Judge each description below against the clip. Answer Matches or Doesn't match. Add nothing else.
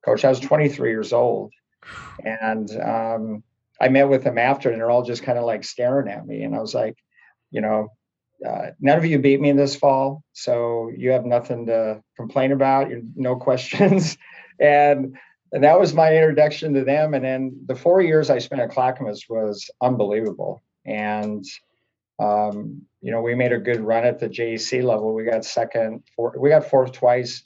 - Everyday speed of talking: Matches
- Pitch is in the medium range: Doesn't match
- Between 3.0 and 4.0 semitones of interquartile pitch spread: Matches